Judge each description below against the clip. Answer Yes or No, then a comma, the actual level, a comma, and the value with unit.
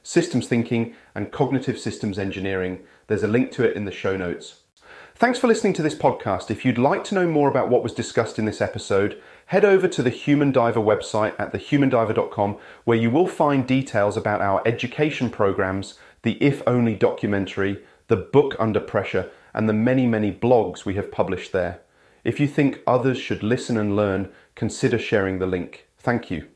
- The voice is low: Yes, low, 115 Hz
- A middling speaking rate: Yes, average, 190 wpm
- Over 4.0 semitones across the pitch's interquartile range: Yes, average, 5.1 semitones